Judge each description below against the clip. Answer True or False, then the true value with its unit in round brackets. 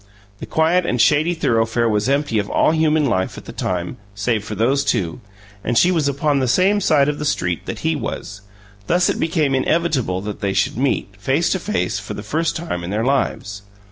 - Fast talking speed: True (210 wpm)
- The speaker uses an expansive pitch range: True (7.2 semitones)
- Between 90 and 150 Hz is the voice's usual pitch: True (135 Hz)